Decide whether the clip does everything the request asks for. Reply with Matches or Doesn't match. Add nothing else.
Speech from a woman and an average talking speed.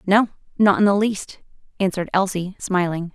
Matches